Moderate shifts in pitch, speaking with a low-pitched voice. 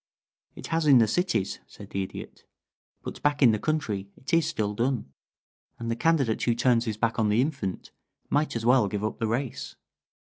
Yes: average, 4.7 semitones; low, 115 Hz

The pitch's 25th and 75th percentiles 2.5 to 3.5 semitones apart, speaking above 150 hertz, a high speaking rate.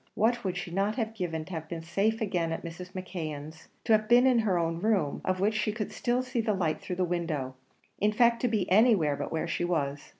No: average, 4.9 semitones; medium, 185 Hz; fast, 240 wpm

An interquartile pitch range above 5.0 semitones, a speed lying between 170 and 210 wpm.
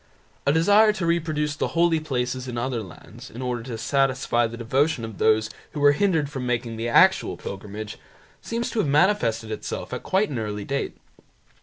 Yes: wide, 5.5 semitones; average, 185 wpm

